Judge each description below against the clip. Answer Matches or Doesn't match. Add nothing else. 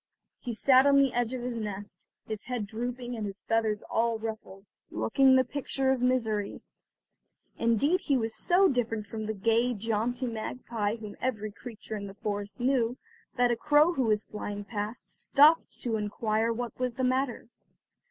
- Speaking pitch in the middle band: Doesn't match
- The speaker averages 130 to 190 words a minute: Matches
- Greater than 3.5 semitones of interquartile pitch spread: Doesn't match